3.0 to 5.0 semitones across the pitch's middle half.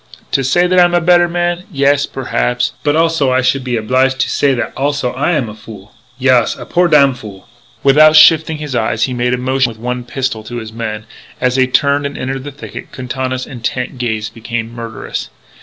Yes: average, 3.3 semitones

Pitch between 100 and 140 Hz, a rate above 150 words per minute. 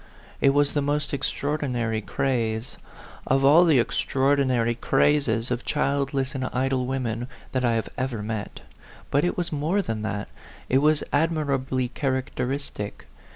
No: low, 135 Hz; average, 145 wpm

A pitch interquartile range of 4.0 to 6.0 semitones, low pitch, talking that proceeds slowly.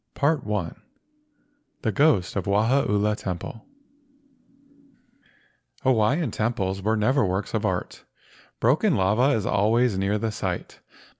Yes: average, 4.4 semitones; low, 110 Hz; slow, 125 wpm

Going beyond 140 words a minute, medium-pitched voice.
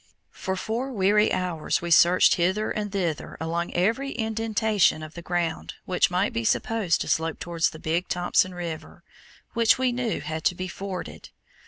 Yes: average, 170 wpm; medium, 180 Hz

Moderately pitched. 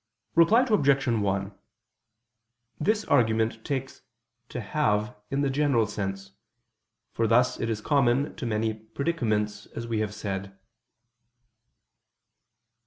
No: low, 115 Hz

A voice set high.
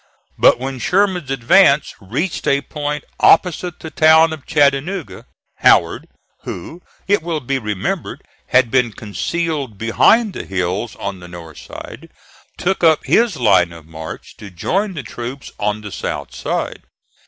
No: low, 135 Hz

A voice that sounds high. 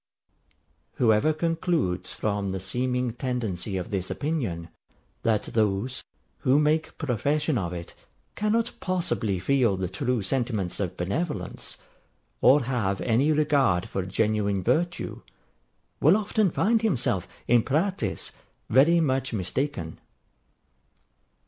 No: low, 125 Hz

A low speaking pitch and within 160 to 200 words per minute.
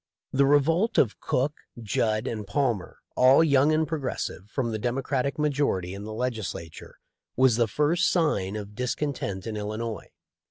No: low, 125 Hz; average, 150 wpm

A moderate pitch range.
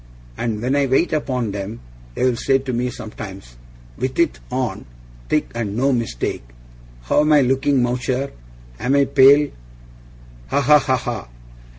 Yes: average, 3.0 semitones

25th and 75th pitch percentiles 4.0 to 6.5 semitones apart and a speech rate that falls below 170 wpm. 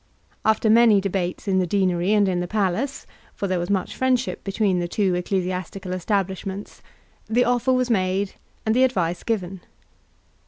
No: average, 3.1 semitones; average, 160 wpm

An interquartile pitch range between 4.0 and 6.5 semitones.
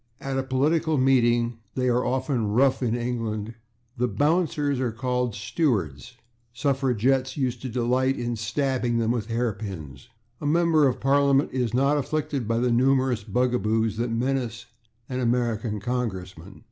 No: average, 2.7 semitones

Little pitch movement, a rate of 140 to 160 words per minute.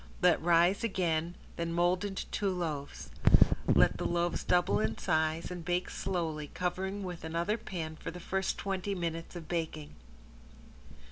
Yes: narrow, 2.2 semitones; average, 150 wpm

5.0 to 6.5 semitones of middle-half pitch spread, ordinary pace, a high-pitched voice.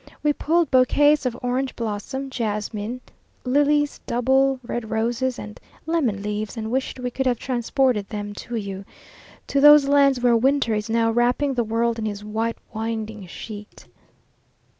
No: average, 3.6 semitones; average, 155 wpm; high, 240 Hz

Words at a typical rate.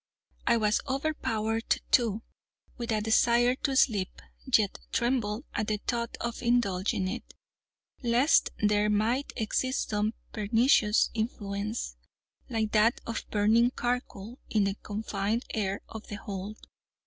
No: slow, 125 wpm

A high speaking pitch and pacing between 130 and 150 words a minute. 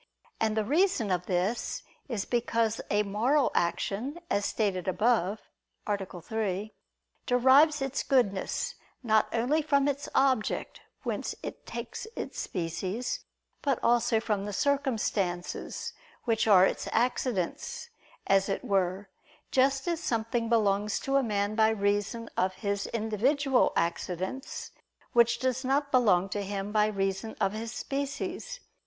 Yes: high, 220 Hz; slow, 135 wpm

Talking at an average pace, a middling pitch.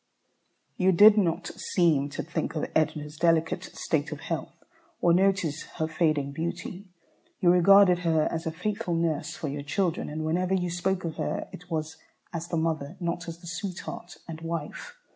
Yes: average, 175 wpm; medium, 170 Hz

